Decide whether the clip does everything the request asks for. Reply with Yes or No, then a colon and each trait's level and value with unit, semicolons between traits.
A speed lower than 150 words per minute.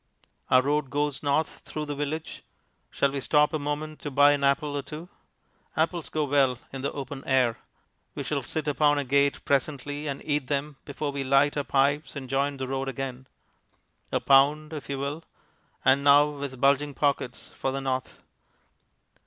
No: average, 180 wpm